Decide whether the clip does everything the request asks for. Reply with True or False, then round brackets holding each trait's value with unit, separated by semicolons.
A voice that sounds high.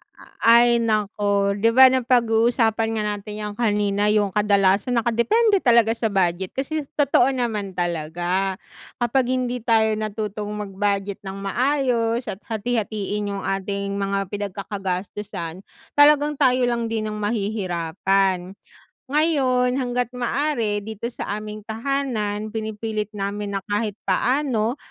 True (215 Hz)